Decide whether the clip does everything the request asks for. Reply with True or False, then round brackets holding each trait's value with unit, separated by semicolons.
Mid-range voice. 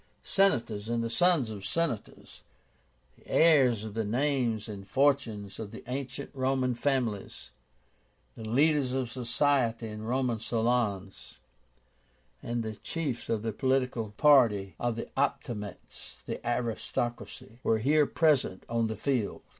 False (120 Hz)